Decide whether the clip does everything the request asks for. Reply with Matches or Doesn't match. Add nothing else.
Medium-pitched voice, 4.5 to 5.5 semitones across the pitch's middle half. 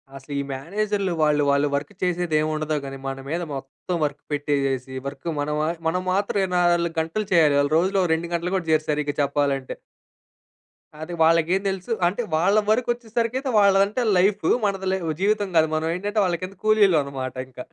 Matches